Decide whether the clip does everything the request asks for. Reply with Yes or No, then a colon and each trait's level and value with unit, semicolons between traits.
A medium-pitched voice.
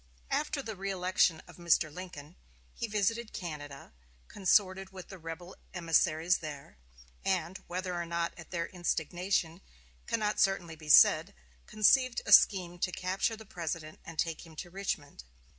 Yes: medium, 175 Hz